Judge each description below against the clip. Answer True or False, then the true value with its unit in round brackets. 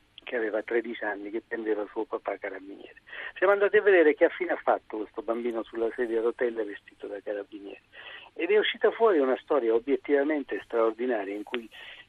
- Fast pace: True (180 wpm)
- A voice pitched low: True (120 Hz)